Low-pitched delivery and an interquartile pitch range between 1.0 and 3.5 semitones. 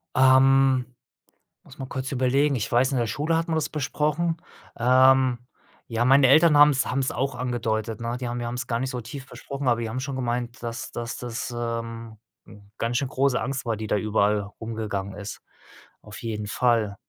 Yes: low, 125 Hz; narrow, 2.6 semitones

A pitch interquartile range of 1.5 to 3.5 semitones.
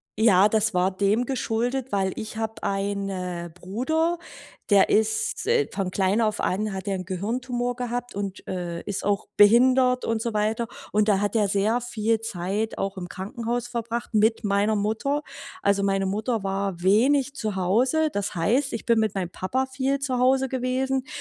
No: average, 3.9 semitones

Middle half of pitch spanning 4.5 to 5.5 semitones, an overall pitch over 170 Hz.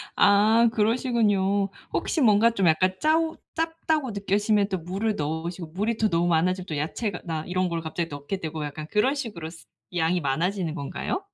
Yes: average, 5.1 semitones; high, 190 Hz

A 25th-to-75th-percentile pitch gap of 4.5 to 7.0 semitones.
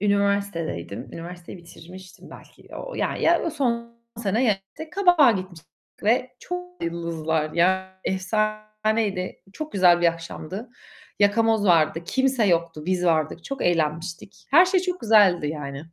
Yes: wide, 5.4 semitones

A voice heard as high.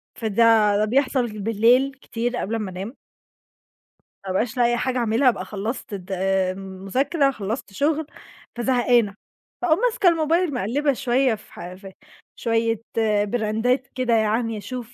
Yes: high, 230 Hz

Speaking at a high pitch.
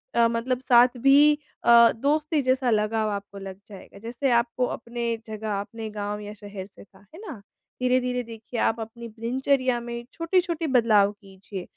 Yes: high, 235 Hz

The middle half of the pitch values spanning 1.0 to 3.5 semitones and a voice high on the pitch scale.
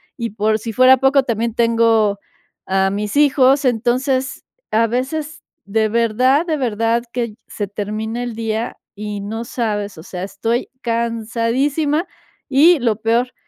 Yes: average, 3.2 semitones; high, 230 Hz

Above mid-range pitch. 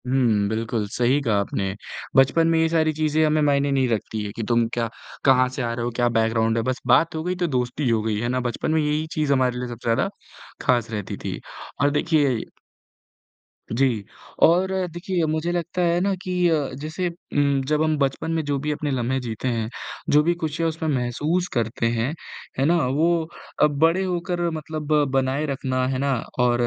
No: medium, 140 Hz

